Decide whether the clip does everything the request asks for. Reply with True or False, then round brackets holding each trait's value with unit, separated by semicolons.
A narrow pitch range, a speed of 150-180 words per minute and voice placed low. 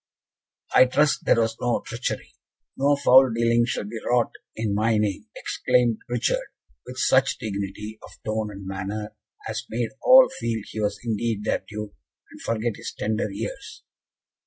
True (2.1 semitones; 160 wpm; 110 Hz)